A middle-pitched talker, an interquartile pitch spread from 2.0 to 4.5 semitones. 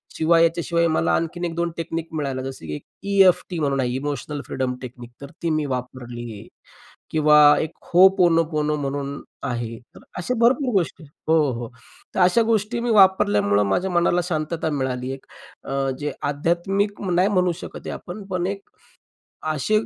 No: medium, 160 Hz; average, 5.0 semitones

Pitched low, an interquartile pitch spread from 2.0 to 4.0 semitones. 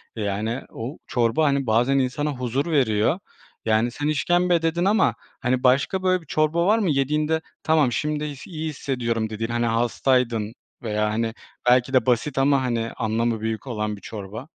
No: low, 125 Hz; average, 5.0 semitones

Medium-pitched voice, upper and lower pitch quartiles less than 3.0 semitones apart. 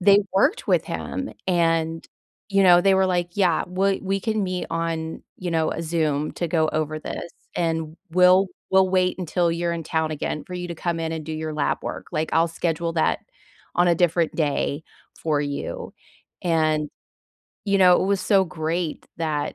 Yes: medium, 170 Hz; narrow, 2.4 semitones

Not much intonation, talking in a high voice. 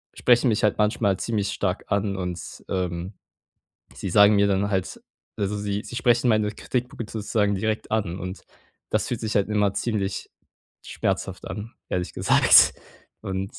No: narrow, 2.2 semitones; low, 100 Hz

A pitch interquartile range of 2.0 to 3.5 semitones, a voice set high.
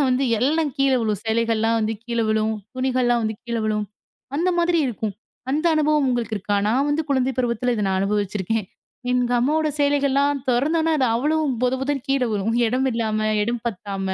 No: average, 4.3 semitones; high, 245 Hz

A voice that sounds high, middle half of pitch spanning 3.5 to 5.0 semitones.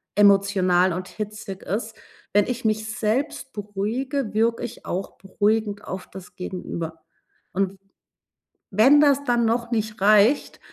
No: high, 210 Hz; average, 3.0 semitones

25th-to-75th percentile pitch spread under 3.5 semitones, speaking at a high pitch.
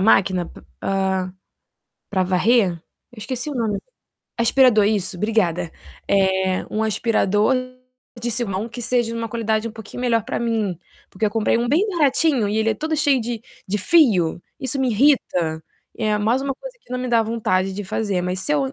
No: average, 4.2 semitones; high, 220 Hz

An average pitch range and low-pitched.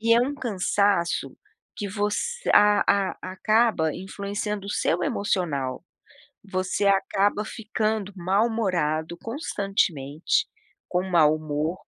No: average, 3.7 semitones; high, 200 Hz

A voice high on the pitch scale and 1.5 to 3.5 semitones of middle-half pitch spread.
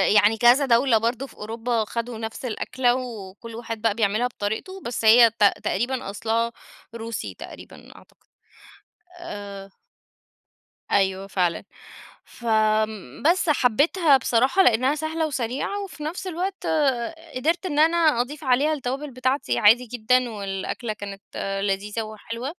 No: high, 235 Hz; average, 4.3 semitones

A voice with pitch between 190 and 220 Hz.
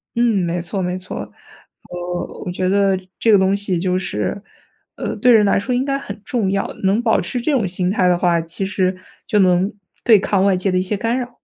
Yes: high, 195 Hz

